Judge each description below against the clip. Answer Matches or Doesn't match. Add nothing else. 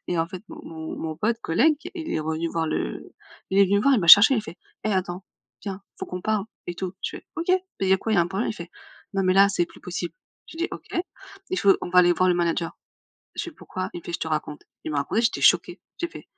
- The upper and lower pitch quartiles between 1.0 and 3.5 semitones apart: Doesn't match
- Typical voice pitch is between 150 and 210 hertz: Matches